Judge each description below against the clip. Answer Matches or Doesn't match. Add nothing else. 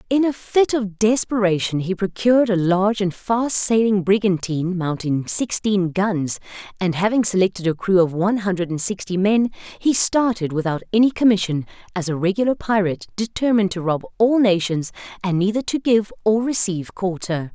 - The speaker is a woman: Matches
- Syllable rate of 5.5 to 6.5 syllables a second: Doesn't match